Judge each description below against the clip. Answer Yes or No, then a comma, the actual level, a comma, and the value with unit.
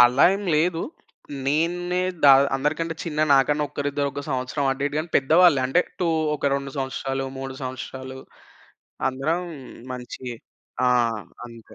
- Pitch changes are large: No, average, 3.5 semitones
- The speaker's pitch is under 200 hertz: Yes, medium, 140 Hz